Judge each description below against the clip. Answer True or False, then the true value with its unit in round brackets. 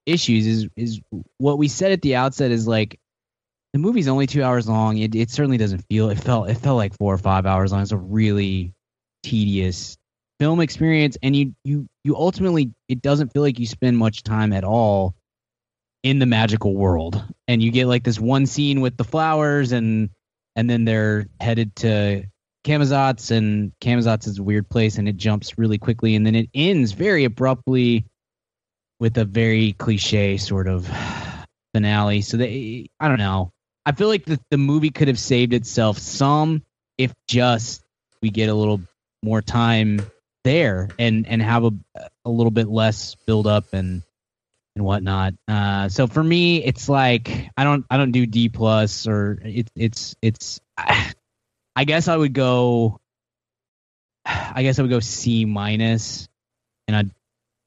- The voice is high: False (115 Hz)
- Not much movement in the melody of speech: False (3.6 semitones)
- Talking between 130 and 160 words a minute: False (175 wpm)